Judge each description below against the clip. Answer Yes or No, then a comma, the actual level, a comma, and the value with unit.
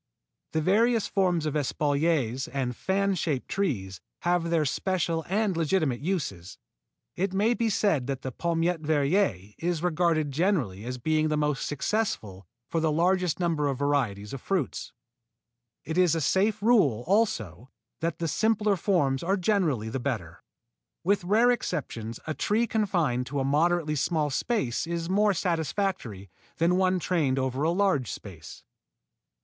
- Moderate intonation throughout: No, wide, 5.9 semitones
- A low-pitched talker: No, medium, 160 Hz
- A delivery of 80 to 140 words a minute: No, average, 155 wpm